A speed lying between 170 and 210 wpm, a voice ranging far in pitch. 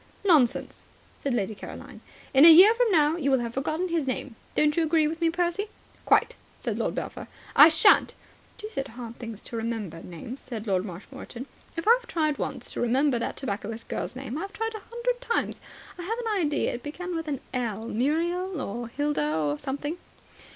Yes: average, 190 wpm; wide, 6.8 semitones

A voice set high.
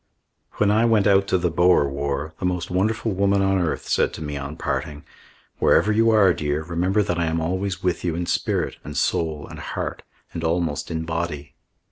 No: very low, 85 Hz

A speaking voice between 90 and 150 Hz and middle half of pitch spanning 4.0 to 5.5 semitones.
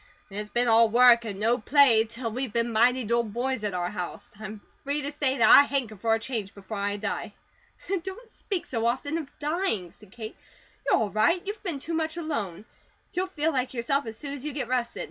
No: high, 240 Hz; average, 4.8 semitones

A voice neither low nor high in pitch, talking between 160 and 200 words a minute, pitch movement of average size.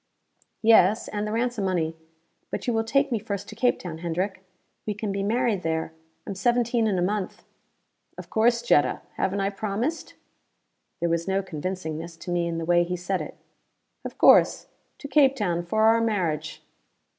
No: high, 195 Hz; average, 180 wpm; average, 4.5 semitones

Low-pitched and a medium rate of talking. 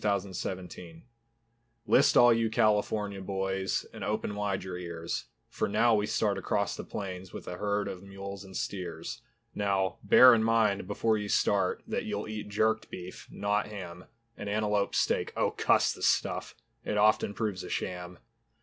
Yes: low, 100 Hz; average, 165 wpm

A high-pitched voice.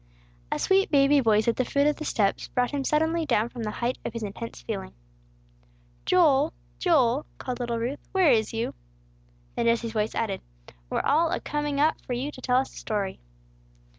Yes: very high, 255 Hz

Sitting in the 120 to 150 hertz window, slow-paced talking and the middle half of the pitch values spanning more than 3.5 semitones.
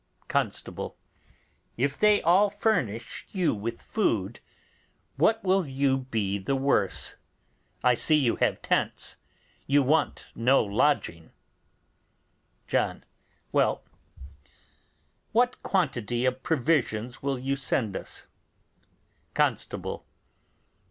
Yes: low, 135 Hz; slow, 100 wpm; wide, 5.6 semitones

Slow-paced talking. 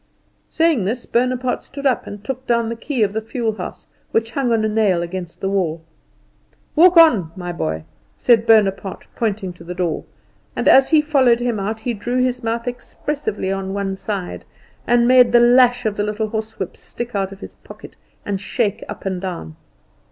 No: average, 190 wpm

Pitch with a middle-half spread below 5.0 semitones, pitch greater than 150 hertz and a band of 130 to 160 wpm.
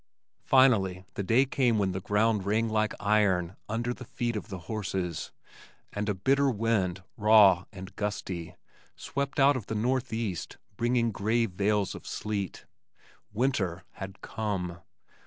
No: average, 3.5 semitones; low, 105 Hz; average, 140 wpm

